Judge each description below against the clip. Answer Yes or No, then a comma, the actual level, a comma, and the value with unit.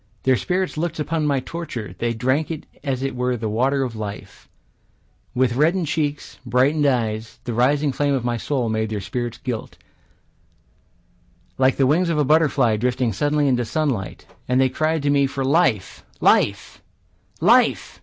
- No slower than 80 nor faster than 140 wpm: No, average, 165 wpm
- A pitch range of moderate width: Yes, average, 3.8 semitones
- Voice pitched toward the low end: Yes, low, 130 Hz